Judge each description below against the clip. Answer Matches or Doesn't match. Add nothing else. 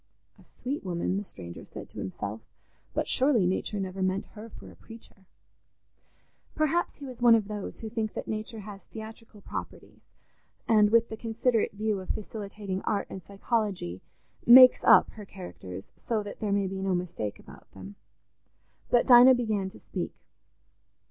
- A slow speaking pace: Doesn't match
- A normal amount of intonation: Matches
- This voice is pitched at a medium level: Doesn't match